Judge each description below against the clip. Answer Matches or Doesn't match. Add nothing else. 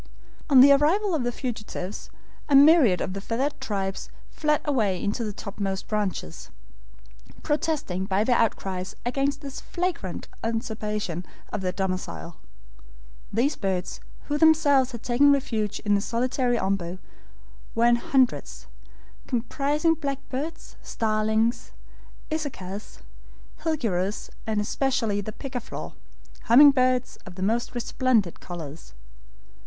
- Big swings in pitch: Matches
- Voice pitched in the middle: Doesn't match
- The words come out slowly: Matches